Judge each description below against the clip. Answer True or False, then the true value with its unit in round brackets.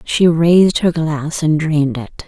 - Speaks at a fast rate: False (185 wpm)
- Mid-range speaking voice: True (160 Hz)